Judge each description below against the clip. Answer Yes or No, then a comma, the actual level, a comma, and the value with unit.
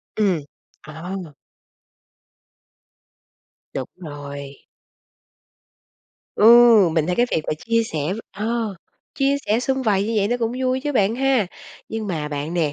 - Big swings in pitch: Yes, wide, 6.8 semitones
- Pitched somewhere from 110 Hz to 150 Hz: No, high, 205 Hz